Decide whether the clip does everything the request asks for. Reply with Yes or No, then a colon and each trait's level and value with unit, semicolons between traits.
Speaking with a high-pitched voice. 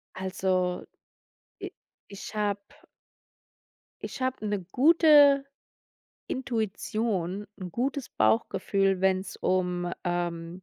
Yes: high, 195 Hz